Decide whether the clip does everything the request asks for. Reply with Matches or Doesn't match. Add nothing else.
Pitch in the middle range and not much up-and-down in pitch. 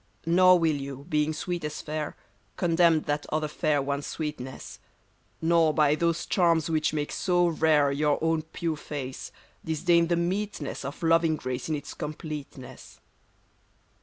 Matches